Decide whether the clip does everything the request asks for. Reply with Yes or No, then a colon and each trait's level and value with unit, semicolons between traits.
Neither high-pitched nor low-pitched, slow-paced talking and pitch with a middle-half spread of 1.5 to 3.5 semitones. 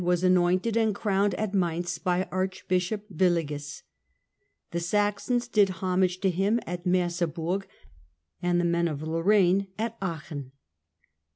Yes: medium, 180 Hz; slow, 125 wpm; narrow, 2.5 semitones